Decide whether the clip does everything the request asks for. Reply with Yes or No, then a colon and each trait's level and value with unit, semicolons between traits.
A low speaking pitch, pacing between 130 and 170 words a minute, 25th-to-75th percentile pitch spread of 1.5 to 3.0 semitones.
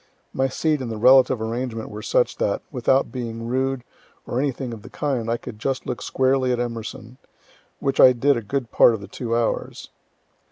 No: low, 125 Hz; average, 195 wpm; narrow, 2.5 semitones